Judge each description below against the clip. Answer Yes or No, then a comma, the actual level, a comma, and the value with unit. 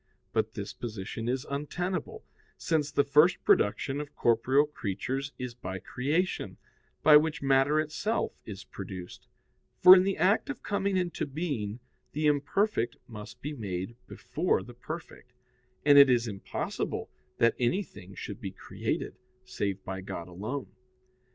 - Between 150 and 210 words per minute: No, average, 140 wpm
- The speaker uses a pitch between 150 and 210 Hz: No, low, 135 Hz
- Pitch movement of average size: No, wide, 6.3 semitones